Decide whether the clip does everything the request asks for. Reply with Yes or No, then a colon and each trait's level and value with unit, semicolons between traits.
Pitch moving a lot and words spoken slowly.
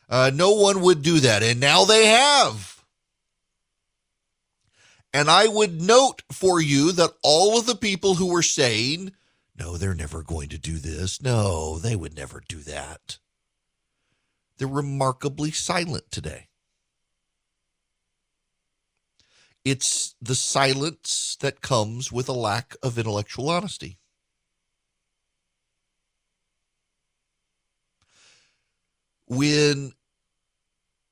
Yes: wide, 8.4 semitones; slow, 100 wpm